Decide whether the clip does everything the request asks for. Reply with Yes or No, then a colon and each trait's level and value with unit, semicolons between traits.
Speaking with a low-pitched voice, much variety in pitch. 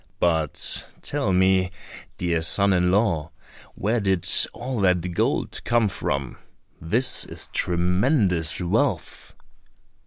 No: very low, 90 Hz; average, 2.9 semitones